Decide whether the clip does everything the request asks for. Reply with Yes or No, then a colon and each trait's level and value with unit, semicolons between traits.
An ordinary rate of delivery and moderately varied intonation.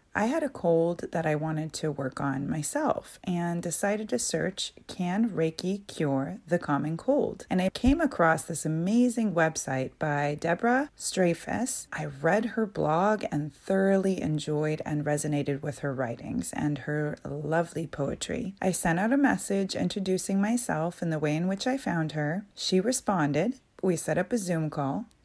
Yes: average, 165 wpm; average, 5.0 semitones